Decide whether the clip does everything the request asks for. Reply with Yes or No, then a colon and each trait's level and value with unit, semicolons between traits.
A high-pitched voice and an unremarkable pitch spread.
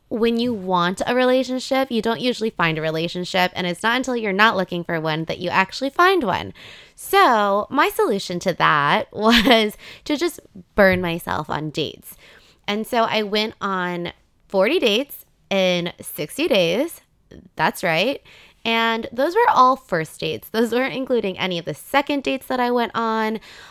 No: high, 225 Hz; wide, 5.7 semitones